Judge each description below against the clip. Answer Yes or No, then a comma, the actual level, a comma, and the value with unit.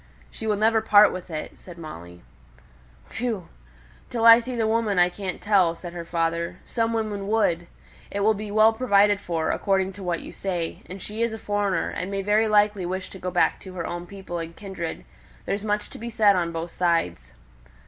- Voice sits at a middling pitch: No, high, 195 Hz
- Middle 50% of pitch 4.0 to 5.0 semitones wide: No, average, 3.6 semitones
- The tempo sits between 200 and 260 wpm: Yes, fast, 205 wpm